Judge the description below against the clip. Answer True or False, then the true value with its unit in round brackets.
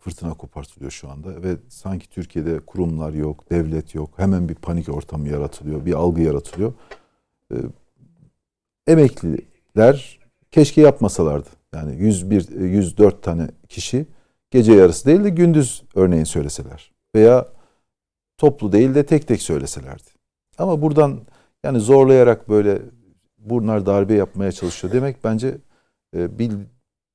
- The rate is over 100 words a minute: True (120 wpm)